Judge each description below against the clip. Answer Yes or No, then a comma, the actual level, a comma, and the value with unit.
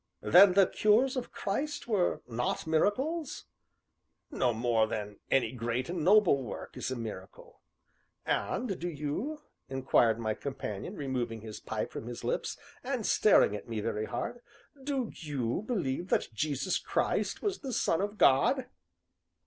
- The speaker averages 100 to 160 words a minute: Yes, average, 150 wpm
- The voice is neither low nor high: Yes, medium, 150 Hz